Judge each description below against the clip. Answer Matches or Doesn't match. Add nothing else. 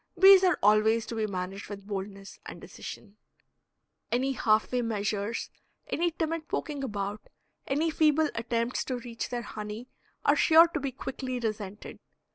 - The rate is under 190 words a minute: Matches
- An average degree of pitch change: Matches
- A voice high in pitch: Matches